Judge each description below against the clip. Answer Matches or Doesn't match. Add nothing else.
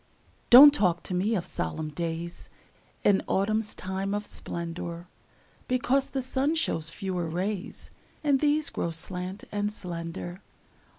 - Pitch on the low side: Doesn't match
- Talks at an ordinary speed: Doesn't match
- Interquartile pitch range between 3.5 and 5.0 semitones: Matches